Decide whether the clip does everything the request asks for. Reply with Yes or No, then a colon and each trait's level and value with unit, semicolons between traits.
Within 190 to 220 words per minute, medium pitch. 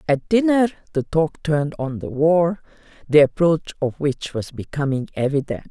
No: average, 160 wpm; medium, 150 Hz